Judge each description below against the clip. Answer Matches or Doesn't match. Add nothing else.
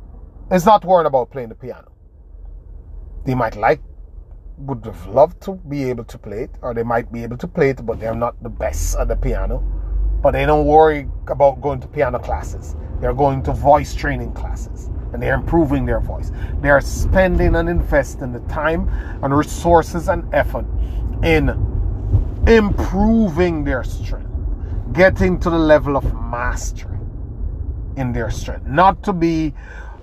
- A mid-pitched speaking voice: Doesn't match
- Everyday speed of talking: Matches